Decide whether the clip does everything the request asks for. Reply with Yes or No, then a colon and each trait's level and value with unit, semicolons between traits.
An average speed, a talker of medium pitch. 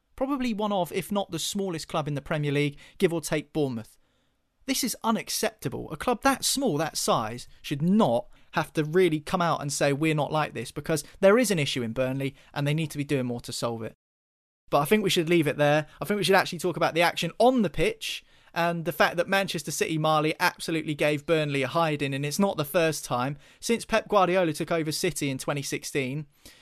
No: fast, 230 wpm; medium, 160 Hz